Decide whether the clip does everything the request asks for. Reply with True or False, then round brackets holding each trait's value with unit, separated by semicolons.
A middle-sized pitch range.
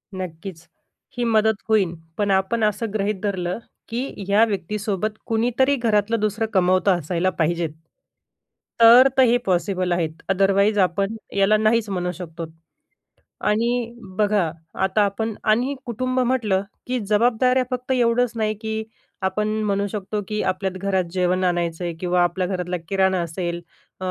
True (3.4 semitones)